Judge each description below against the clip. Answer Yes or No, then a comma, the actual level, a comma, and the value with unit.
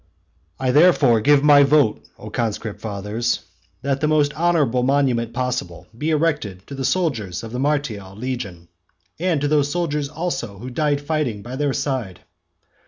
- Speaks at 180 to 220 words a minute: No, average, 165 wpm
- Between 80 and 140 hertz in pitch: Yes, low, 135 Hz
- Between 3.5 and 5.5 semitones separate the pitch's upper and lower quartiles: Yes, average, 4.6 semitones